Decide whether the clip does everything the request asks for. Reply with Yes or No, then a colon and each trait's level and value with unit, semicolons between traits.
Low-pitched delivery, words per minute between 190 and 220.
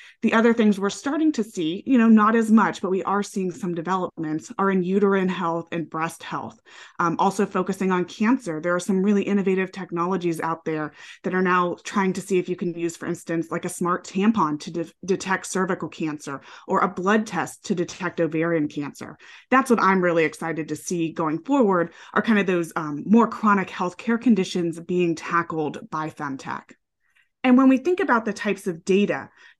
No: medium, 185 Hz; average, 200 wpm